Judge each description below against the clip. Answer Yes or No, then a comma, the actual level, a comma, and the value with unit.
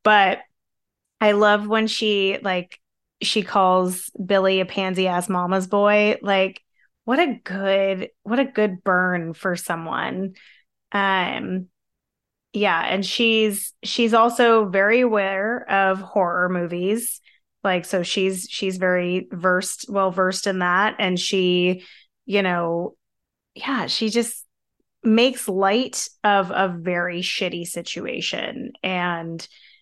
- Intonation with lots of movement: No, average, 2.7 semitones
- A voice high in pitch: Yes, high, 195 Hz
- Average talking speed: No, slow, 120 wpm